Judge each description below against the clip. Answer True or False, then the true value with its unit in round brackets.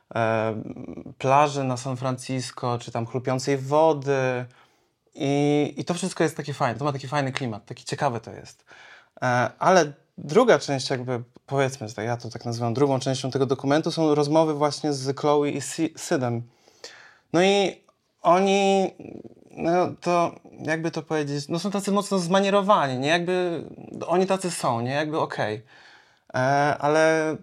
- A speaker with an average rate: True (145 wpm)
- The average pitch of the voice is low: False (145 Hz)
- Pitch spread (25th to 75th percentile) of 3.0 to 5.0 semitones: True (4.0 semitones)